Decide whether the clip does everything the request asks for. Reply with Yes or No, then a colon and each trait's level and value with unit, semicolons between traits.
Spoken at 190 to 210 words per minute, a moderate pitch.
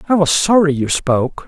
Yes: fast, 205 wpm; medium, 160 Hz